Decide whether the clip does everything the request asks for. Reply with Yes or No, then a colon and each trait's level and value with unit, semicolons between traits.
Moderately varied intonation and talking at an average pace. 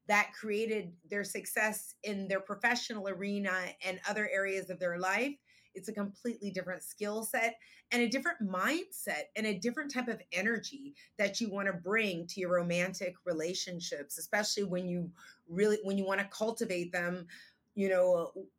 Yes: average, 3.1 semitones; average, 165 wpm